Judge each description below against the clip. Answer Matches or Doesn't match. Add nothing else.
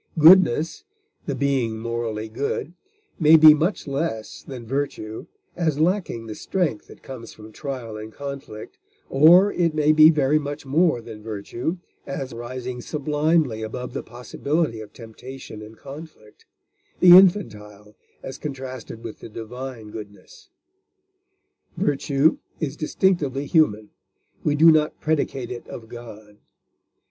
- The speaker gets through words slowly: Matches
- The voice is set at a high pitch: Doesn't match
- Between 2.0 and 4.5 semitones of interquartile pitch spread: Doesn't match